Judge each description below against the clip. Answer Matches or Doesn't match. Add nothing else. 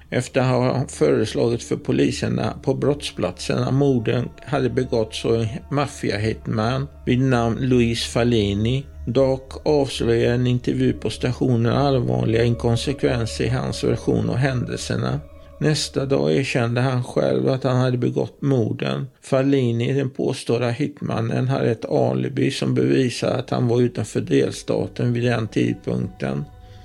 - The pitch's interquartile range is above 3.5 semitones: Matches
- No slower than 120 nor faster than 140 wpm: Matches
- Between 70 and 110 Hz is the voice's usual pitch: Doesn't match